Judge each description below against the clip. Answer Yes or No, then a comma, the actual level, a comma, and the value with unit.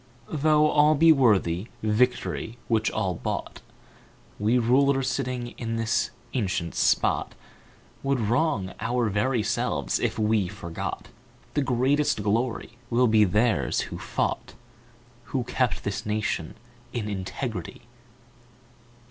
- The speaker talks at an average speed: No, slow, 115 wpm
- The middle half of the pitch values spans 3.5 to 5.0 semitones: Yes, average, 3.8 semitones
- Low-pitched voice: Yes, low, 115 Hz